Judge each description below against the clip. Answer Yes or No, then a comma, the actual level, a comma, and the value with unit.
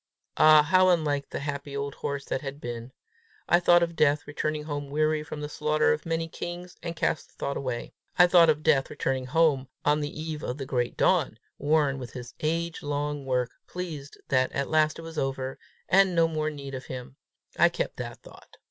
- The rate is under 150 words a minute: No, fast, 205 wpm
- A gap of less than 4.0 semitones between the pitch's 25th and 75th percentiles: Yes, average, 3.0 semitones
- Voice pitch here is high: No, medium, 150 Hz